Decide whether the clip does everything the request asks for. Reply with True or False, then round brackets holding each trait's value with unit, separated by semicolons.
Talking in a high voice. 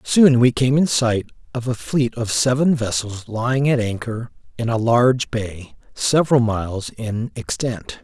False (115 Hz)